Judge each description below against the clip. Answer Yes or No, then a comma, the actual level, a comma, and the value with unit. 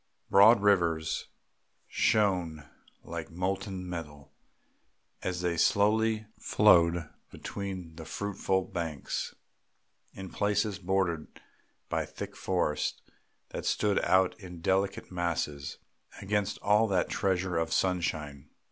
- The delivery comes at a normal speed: No, slow, 100 wpm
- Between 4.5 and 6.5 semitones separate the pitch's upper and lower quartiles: No, average, 3.0 semitones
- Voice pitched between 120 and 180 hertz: No, very low, 90 Hz